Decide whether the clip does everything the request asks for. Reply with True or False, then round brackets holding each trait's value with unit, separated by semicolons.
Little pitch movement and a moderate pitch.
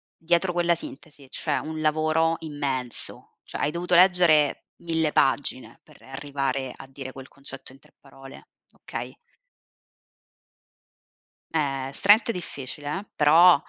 False (3.9 semitones; 150 Hz)